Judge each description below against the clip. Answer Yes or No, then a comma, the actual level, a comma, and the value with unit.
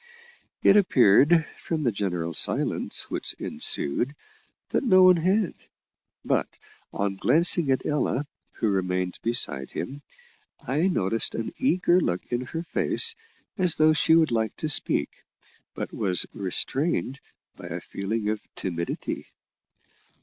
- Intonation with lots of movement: Yes, wide, 9.0 semitones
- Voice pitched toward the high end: No, low, 130 Hz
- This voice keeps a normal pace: No, slow, 130 wpm